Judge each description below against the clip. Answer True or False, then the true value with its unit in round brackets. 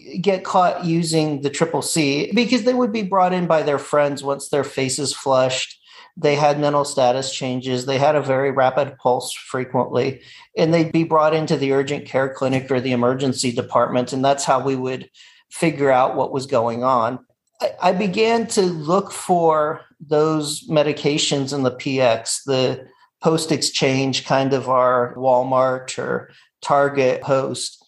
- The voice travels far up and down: False (3.7 semitones)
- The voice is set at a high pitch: False (140 Hz)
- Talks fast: False (160 wpm)